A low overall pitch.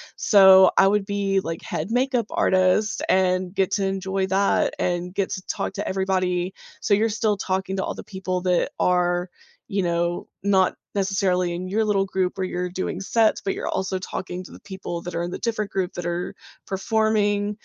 No: high, 190 Hz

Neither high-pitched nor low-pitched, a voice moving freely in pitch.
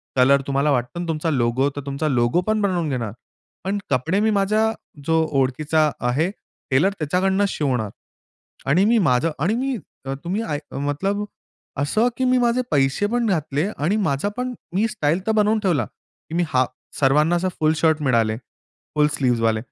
Yes: medium, 155 Hz; wide, 6.5 semitones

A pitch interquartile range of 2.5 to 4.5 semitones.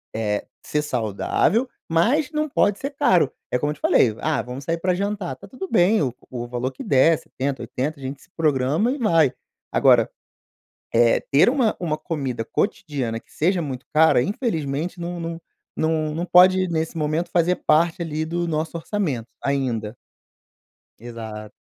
No: average, 5.3 semitones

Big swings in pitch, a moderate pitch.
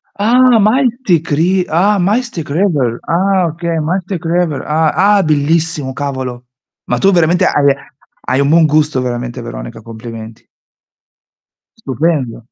Yes: wide, 6.0 semitones; medium, 160 Hz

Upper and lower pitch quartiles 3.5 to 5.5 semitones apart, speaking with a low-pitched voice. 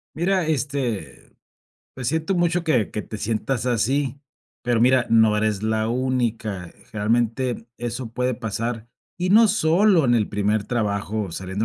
Yes: average, 4.2 semitones; low, 120 Hz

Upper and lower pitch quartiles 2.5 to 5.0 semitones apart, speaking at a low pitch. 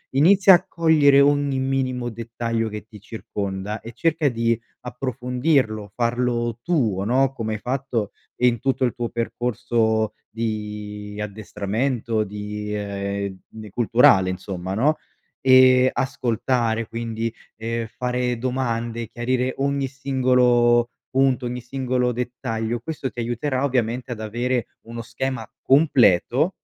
Yes: average, 2.9 semitones; low, 120 Hz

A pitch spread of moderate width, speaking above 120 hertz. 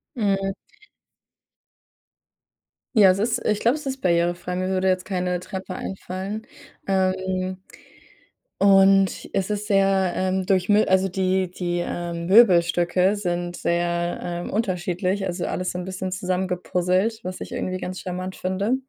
No: narrow, 1.4 semitones; medium, 185 Hz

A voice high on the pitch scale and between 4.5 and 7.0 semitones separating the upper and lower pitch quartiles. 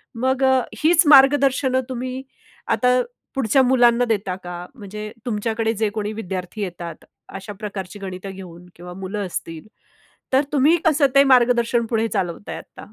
Yes: high, 225 Hz; average, 5.2 semitones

